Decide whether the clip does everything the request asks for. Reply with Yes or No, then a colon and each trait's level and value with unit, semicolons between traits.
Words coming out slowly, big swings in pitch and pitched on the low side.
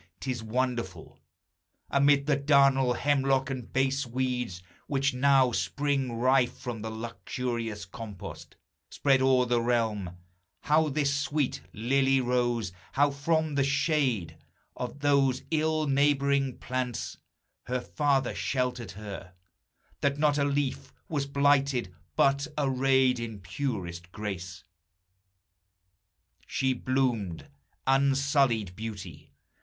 No: slow, 110 wpm; average, 3.2 semitones; low, 130 Hz